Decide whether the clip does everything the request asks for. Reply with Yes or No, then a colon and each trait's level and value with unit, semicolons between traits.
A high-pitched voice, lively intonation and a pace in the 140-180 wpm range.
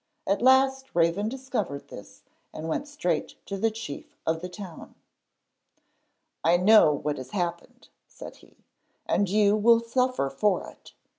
Yes: high, 205 Hz; wide, 5.9 semitones; average, 145 wpm